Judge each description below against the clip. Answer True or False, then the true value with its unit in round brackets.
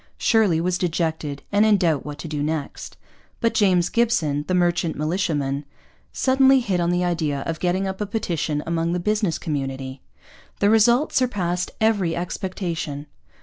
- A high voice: False (175 Hz)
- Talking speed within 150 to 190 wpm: True (155 wpm)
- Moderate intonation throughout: True (4.7 semitones)